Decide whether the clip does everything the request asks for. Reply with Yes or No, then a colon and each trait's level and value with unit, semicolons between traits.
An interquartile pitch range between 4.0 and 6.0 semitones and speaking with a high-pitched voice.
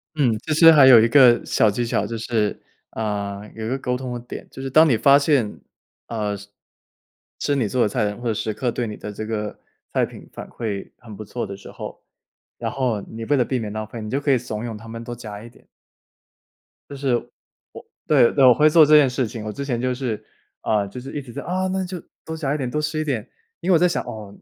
No: average, 4.4 semitones; low, 120 Hz